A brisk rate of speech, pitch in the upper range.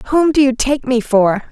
Yes: fast, 235 wpm; very high, 255 Hz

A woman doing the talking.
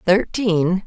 Yes: female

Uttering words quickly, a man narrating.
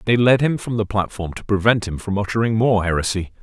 Yes: fast, 230 wpm; male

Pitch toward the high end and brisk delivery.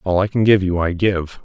No: very low, 95 Hz; fast, 290 wpm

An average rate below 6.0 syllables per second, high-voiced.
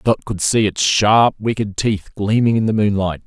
No: 4.5 syllables/s; low, 105 Hz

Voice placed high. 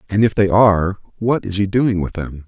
No: low, 100 Hz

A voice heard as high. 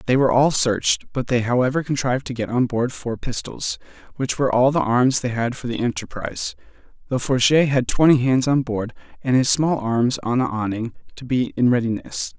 No: low, 125 Hz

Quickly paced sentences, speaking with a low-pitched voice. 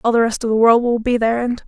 No: fast, 360 wpm; high, 230 Hz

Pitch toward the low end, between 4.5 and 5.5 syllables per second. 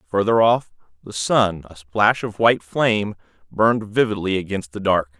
Yes: low, 100 Hz; 5.0 syllables/s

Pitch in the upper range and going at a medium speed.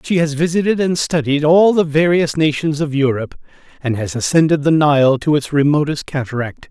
No: medium, 150 Hz; average, 180 wpm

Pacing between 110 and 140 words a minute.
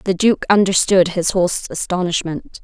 Yes: slow, 135 wpm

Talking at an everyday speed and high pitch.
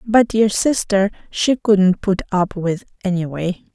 Yes: average, 145 wpm; high, 195 Hz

